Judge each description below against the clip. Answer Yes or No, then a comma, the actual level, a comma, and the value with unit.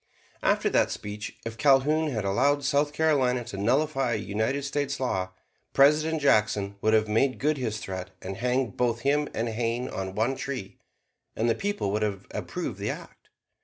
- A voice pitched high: No, low, 125 Hz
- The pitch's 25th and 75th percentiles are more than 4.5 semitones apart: Yes, average, 4.9 semitones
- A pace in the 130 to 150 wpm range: No, average, 175 wpm